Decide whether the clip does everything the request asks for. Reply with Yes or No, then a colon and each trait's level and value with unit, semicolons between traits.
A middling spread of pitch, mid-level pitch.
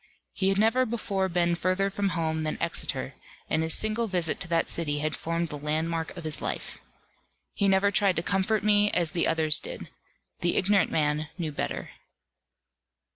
Yes: average, 3.8 semitones; medium, 175 Hz